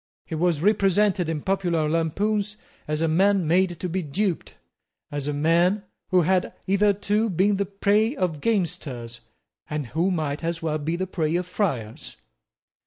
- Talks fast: No, average, 160 wpm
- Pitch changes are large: No, average, 4.0 semitones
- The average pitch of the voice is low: No, medium, 175 Hz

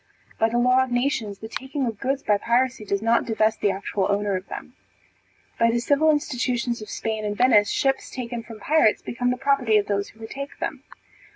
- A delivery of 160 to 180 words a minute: No, fast, 205 wpm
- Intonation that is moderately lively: Yes, average, 3.4 semitones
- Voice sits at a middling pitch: No, high, 235 Hz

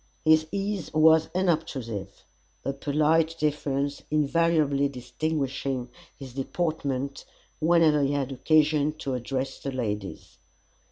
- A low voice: No, medium, 145 Hz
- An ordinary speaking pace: No, slow, 105 wpm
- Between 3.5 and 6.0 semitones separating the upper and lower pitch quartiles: No, average, 2.8 semitones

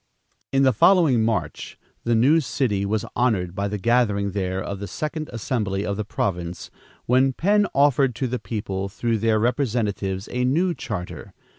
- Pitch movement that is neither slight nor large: Yes, average, 4.6 semitones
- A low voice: Yes, low, 115 Hz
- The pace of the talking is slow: No, average, 165 wpm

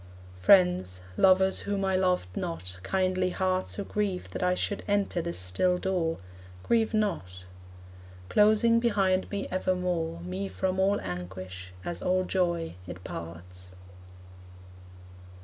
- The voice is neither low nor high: Yes, medium, 180 Hz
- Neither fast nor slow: No, slow, 125 wpm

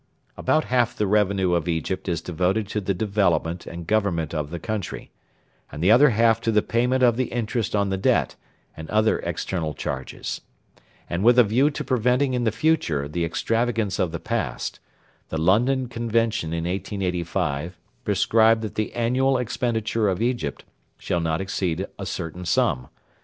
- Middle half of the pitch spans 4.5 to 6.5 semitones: Yes, average, 5.2 semitones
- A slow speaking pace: No, average, 170 wpm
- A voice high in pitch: No, low, 105 Hz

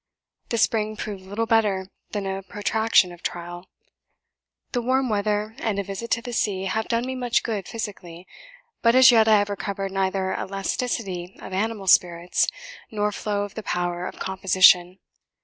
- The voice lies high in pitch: Yes, high, 200 Hz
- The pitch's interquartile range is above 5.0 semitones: No, average, 2.9 semitones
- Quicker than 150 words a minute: Yes, average, 165 wpm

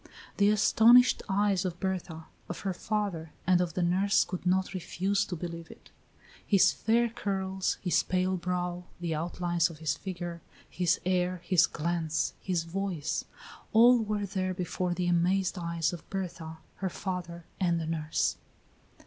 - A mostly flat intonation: Yes, narrow, 2.2 semitones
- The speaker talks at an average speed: Yes, average, 155 wpm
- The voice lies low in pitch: No, medium, 180 Hz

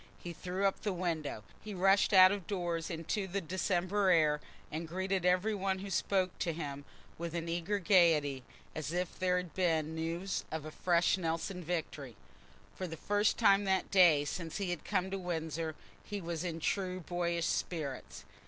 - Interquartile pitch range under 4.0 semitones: Yes, average, 2.7 semitones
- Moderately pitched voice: Yes, medium, 175 Hz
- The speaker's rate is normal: Yes, average, 180 wpm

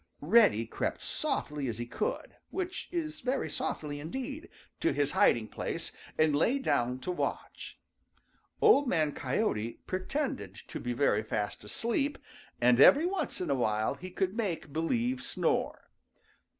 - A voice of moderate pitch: Yes, medium, 170 Hz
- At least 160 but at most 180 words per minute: No, average, 145 wpm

